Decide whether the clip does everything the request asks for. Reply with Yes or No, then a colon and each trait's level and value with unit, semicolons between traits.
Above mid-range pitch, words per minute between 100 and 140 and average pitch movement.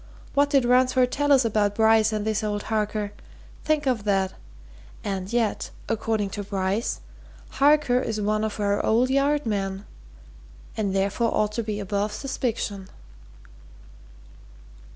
Yes: high, 215 Hz; slow, 135 wpm; average, 3.4 semitones